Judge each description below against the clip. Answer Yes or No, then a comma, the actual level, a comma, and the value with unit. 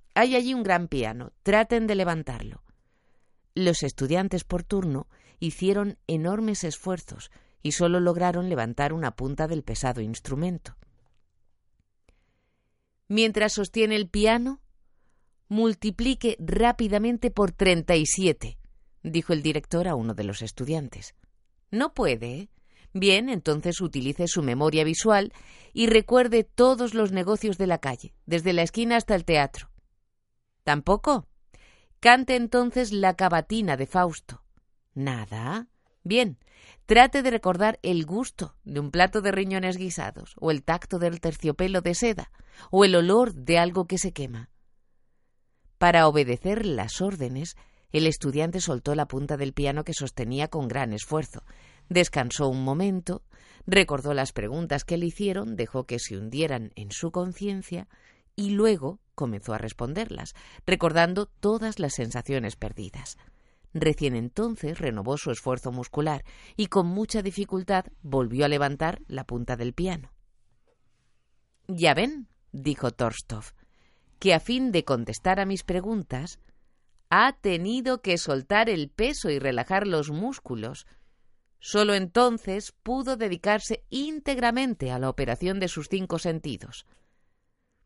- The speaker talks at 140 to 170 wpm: No, average, 130 wpm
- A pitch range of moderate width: No, wide, 7.3 semitones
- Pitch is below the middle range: No, medium, 170 Hz